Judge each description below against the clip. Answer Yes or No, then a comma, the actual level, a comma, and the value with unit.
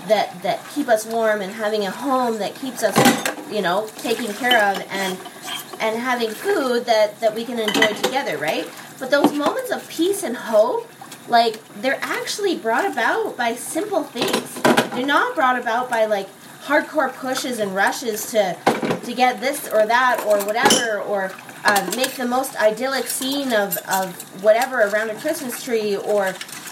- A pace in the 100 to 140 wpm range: No, average, 170 wpm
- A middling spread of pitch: Yes, average, 3.9 semitones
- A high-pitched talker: Yes, high, 235 Hz